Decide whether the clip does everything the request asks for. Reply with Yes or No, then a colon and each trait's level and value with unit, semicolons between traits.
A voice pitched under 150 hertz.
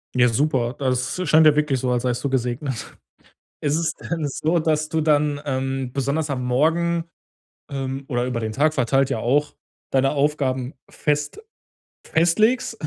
Yes: medium, 140 Hz